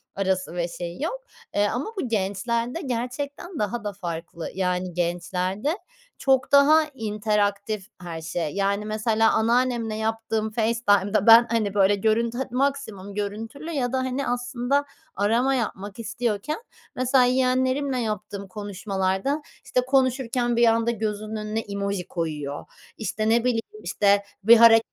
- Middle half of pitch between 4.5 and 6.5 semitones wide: No, average, 3.7 semitones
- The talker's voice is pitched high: Yes, high, 220 Hz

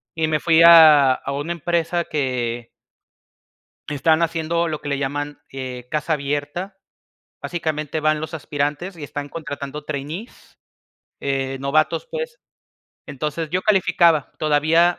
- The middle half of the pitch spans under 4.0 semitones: Yes, average, 2.9 semitones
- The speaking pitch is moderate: Yes, medium, 155 Hz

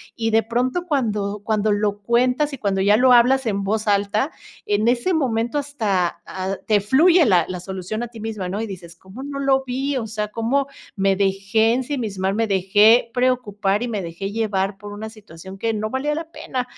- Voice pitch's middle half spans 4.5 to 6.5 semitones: No, average, 4.1 semitones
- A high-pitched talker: Yes, high, 220 Hz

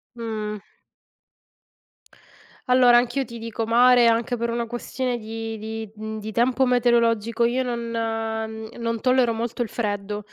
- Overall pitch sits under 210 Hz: No, high, 230 Hz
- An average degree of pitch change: No, narrow, 1.5 semitones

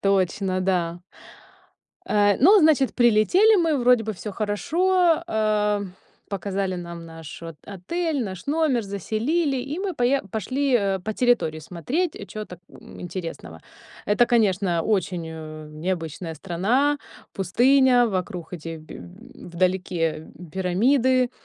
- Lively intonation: Yes, wide, 6.5 semitones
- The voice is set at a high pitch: Yes, high, 205 Hz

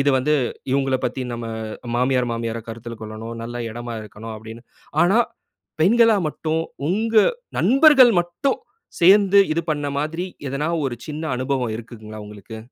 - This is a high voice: No, low, 135 Hz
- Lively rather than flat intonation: Yes, wide, 6.9 semitones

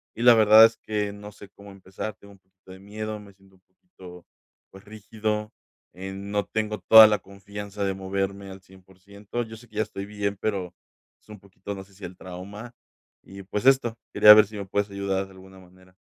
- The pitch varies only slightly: Yes, narrow, 1.8 semitones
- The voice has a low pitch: Yes, low, 100 Hz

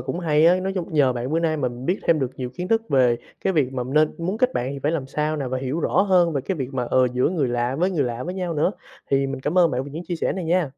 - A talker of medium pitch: Yes, medium, 150 Hz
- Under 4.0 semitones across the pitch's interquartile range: No, average, 5.1 semitones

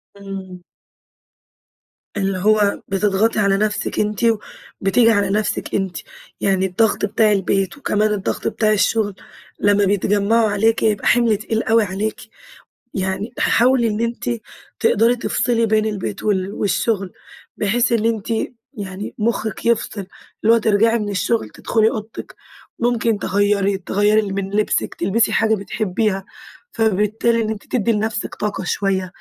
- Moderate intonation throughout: No, narrow, 2.3 semitones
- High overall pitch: Yes, high, 210 Hz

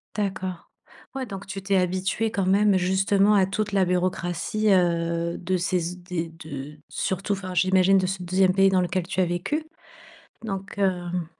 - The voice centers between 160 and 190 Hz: Yes, medium, 185 Hz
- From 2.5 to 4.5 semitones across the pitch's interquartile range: No, narrow, 1.7 semitones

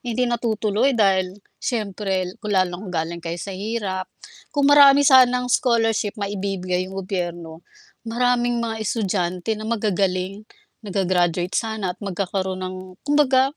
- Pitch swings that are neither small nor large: Yes, average, 4.0 semitones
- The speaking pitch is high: Yes, high, 200 Hz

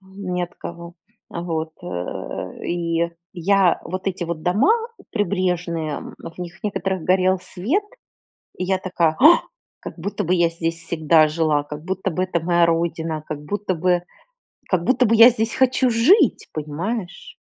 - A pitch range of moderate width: Yes, average, 3.0 semitones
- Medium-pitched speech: Yes, medium, 180 Hz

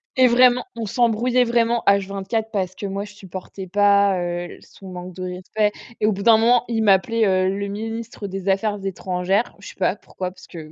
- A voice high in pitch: Yes, high, 200 Hz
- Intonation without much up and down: No, average, 3.2 semitones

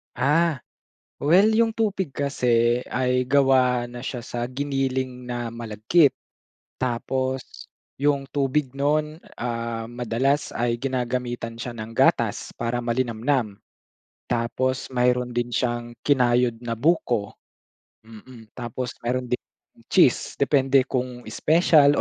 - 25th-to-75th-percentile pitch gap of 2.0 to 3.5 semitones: Yes, narrow, 2.5 semitones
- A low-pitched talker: Yes, low, 125 Hz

